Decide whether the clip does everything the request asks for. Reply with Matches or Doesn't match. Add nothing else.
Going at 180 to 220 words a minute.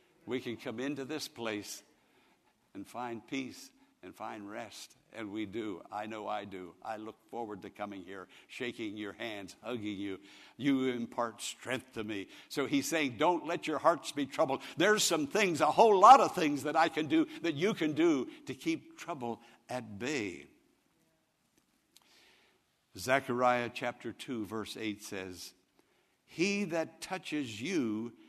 Doesn't match